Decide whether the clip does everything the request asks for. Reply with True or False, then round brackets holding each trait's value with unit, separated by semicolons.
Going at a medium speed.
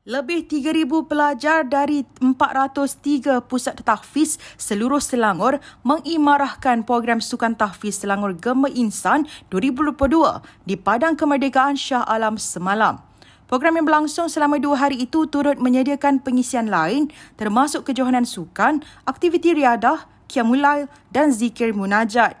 True (115 wpm)